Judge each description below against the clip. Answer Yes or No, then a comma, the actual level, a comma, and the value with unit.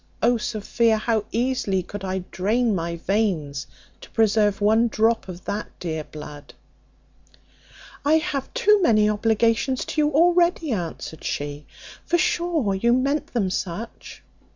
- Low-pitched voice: No, high, 220 Hz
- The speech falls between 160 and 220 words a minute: No, slow, 135 wpm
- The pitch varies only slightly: No, wide, 5.5 semitones